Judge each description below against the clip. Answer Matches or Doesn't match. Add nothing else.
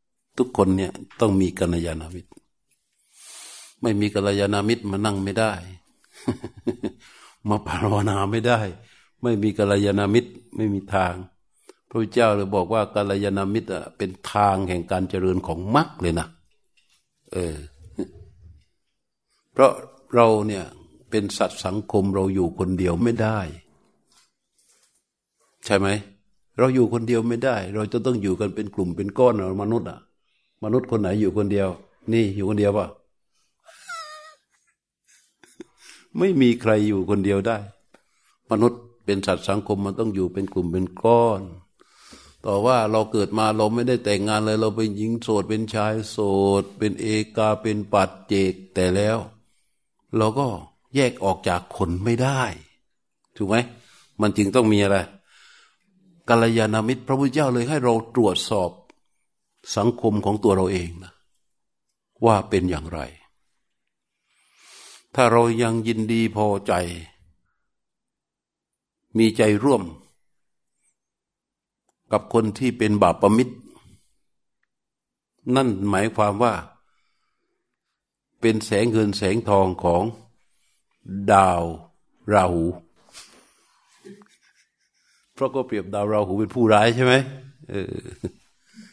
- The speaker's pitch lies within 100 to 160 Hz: Matches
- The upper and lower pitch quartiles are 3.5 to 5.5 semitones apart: Doesn't match